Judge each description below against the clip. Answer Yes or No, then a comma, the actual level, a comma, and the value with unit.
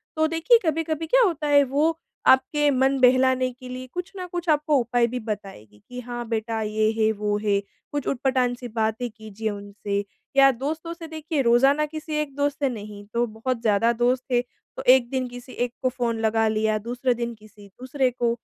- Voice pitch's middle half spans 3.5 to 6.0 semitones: Yes, average, 4.5 semitones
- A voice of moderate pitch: No, high, 245 Hz